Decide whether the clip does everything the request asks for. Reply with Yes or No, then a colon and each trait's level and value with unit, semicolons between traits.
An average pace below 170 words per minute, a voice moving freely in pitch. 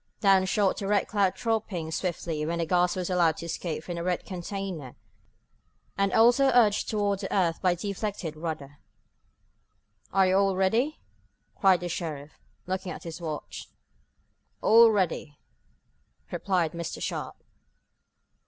No: average, 145 wpm; average, 3.1 semitones